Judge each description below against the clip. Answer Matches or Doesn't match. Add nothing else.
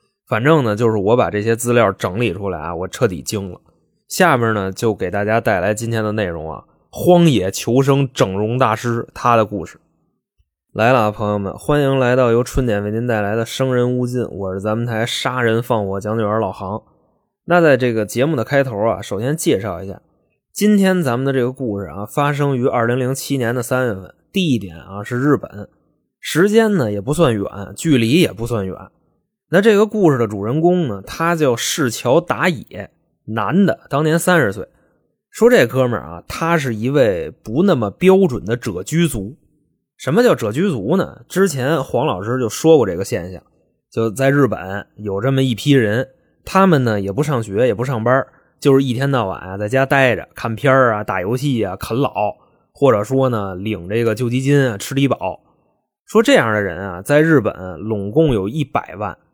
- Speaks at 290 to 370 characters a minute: Doesn't match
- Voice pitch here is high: Doesn't match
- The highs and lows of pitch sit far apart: Doesn't match